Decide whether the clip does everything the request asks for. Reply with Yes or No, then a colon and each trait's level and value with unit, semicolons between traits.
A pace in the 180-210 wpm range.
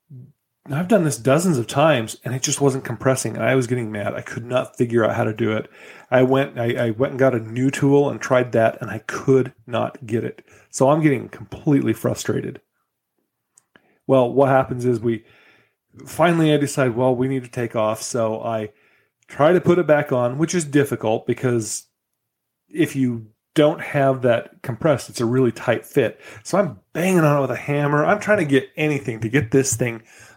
Yes: fast, 205 wpm